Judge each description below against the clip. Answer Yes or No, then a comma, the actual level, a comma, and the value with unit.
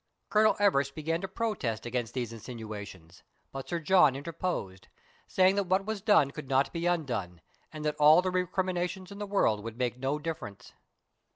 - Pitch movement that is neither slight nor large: No, wide, 7.2 semitones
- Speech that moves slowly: No, average, 175 wpm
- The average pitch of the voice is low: No, medium, 155 Hz